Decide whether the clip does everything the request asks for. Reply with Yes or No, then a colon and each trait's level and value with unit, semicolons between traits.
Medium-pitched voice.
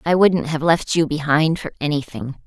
Yes: medium, 150 Hz